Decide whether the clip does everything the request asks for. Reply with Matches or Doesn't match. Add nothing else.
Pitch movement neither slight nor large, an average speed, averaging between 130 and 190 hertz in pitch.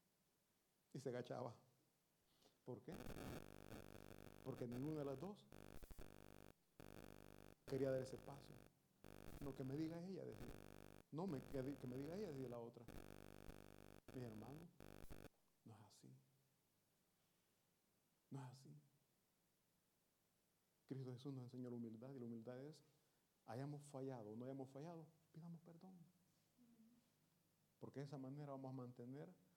Matches